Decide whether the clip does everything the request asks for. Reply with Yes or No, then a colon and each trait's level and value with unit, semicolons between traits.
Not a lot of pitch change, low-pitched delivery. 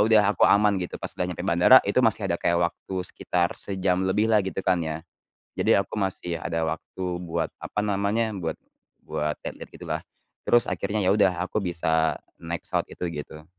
No: average, 3.1 semitones; very low, 95 Hz